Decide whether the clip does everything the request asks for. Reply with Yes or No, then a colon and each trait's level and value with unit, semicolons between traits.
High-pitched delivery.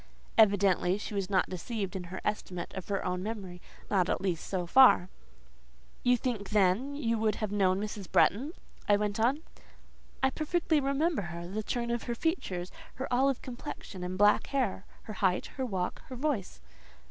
Yes: high, 210 Hz